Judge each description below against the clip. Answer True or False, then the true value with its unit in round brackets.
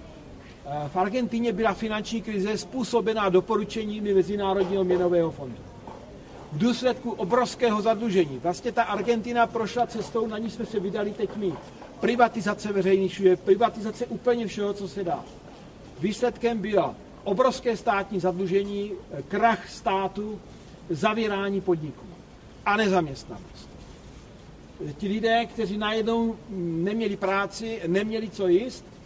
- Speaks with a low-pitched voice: False (205 Hz)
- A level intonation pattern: False (3.1 semitones)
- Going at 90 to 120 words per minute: True (110 wpm)